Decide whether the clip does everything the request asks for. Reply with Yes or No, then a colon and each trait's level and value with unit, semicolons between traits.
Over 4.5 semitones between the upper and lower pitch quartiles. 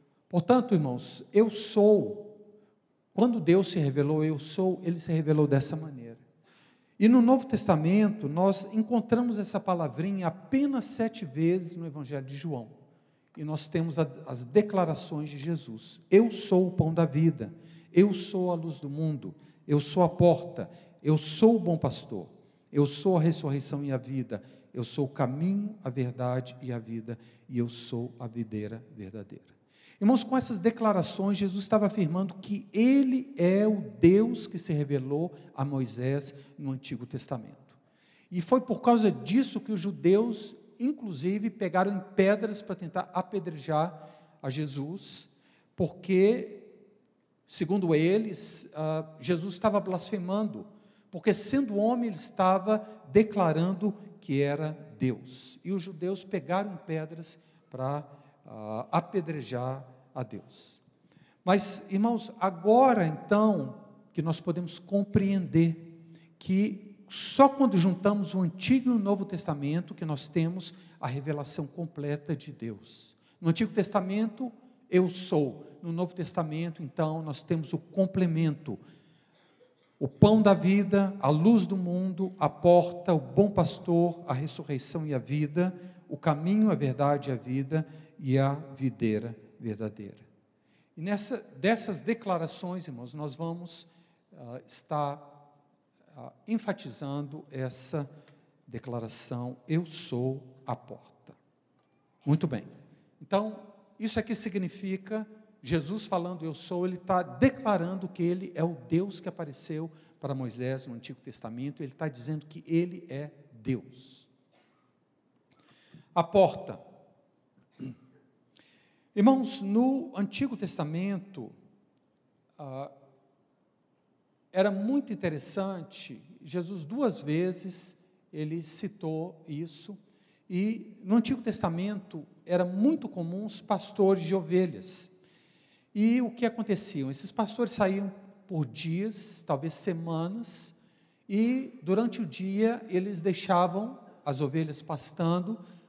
Yes: wide, 5.4 semitones